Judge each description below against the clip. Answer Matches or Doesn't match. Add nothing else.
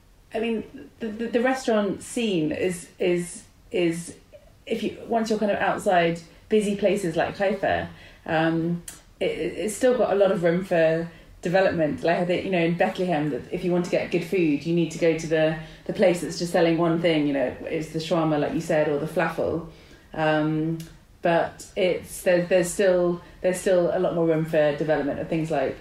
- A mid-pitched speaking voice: Matches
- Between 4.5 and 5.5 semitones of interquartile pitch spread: Doesn't match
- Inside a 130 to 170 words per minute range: Doesn't match